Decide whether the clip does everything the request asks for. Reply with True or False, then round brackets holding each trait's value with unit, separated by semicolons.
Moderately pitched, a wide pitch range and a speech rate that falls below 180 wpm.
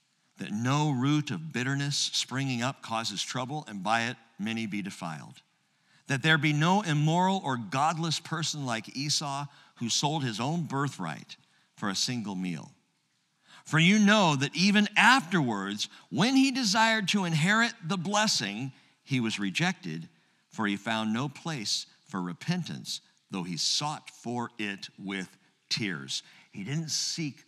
True (145 Hz; 6.5 semitones; 145 wpm)